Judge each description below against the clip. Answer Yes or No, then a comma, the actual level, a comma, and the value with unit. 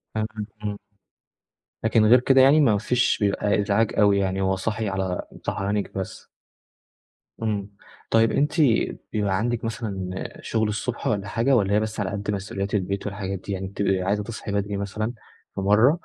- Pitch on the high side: No, low, 105 Hz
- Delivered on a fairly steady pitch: Yes, narrow, 2.2 semitones